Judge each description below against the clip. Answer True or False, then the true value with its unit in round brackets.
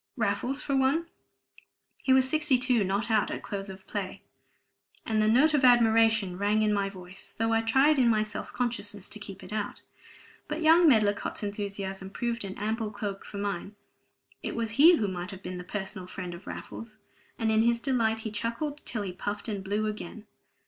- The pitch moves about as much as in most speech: True (3.0 semitones)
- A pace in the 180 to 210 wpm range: True (190 wpm)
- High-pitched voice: True (215 Hz)